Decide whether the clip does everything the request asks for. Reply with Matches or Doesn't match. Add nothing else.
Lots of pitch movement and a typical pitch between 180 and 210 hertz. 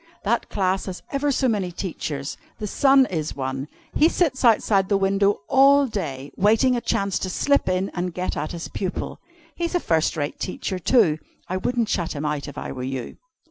Matches